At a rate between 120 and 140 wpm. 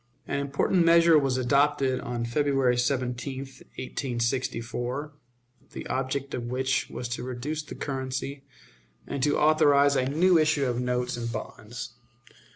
Yes: slow, 135 wpm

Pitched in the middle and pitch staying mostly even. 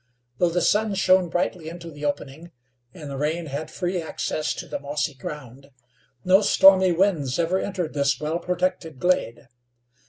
No: medium, 165 Hz; average, 3.8 semitones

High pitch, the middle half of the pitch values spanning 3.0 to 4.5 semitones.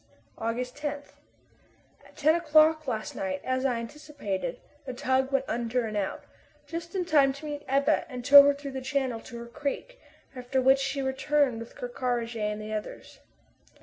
Yes: very high, 265 Hz; average, 3.5 semitones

